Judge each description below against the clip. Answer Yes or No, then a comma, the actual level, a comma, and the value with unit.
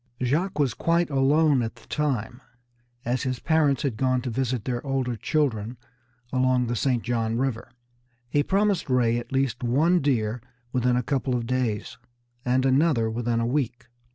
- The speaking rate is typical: Yes, average, 165 wpm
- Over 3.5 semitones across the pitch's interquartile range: No, average, 2.8 semitones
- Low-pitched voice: Yes, low, 130 Hz